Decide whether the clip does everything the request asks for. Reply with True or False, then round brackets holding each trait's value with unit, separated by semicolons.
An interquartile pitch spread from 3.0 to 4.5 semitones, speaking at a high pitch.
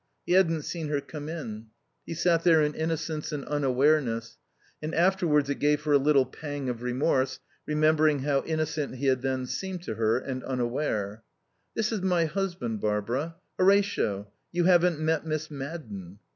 False (4.1 semitones; 150 Hz)